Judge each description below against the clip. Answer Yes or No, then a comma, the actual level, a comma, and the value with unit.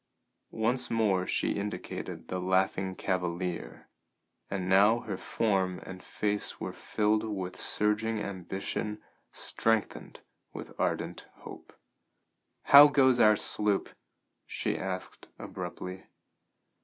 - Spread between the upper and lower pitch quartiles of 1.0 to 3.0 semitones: Yes, average, 2.7 semitones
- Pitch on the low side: Yes, low, 100 Hz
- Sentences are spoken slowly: Yes, slow, 105 wpm